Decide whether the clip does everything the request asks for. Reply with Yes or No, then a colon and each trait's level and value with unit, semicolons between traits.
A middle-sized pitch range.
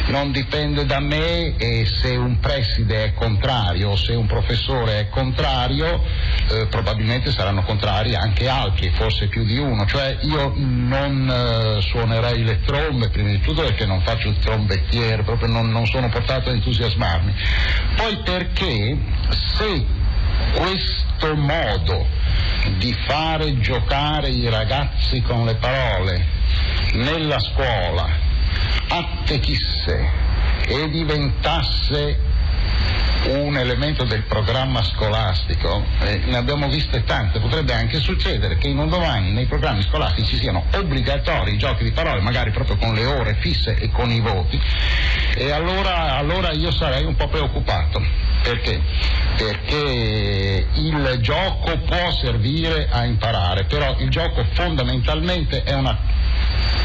No: wide, 5.7 semitones